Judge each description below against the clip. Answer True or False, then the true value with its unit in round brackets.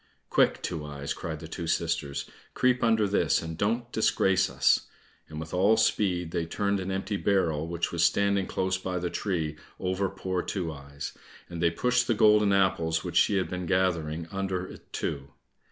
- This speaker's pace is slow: False (185 wpm)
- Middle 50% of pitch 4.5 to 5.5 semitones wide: False (3.4 semitones)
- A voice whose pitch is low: True (90 Hz)